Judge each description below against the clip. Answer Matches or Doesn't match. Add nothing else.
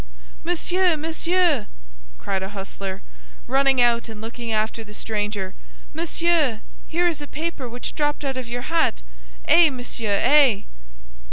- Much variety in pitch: Matches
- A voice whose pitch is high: Matches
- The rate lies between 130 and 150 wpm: Matches